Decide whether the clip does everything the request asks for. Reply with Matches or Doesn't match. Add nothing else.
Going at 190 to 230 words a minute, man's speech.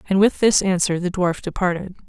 Doesn't match